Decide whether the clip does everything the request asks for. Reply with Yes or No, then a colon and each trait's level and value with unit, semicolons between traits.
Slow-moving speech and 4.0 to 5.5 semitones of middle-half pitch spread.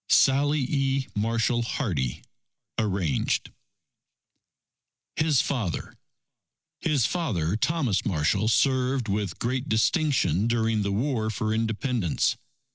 Yes: slow, 95 wpm; average, 4.9 semitones